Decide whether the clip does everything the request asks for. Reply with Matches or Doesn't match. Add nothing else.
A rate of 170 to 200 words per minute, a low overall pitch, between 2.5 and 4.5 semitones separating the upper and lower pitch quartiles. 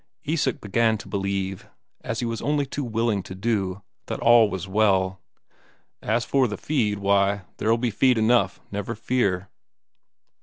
Doesn't match